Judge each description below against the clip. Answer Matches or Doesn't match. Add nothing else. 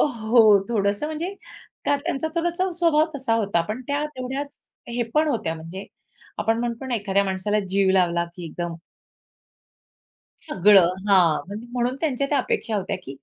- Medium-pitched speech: Doesn't match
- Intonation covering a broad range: Matches